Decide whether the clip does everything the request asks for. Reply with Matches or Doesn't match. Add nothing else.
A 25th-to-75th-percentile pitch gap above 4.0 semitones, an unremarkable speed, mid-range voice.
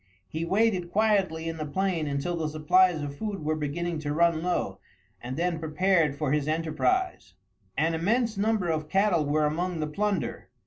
Doesn't match